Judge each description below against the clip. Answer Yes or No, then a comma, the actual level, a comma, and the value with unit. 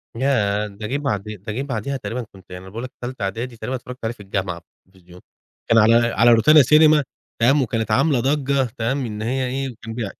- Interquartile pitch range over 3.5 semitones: Yes, average, 4.0 semitones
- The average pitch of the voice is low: Yes, low, 115 Hz